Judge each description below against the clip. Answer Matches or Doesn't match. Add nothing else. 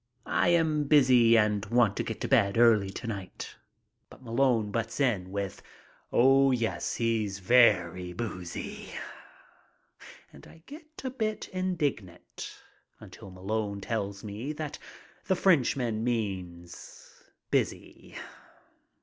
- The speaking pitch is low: Matches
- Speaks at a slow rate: Matches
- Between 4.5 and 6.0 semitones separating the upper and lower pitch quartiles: Matches